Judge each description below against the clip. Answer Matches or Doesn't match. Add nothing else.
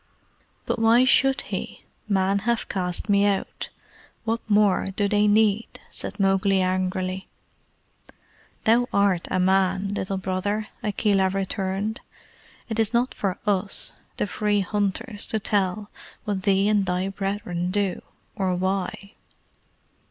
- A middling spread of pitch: Doesn't match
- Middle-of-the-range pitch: Doesn't match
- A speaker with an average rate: Doesn't match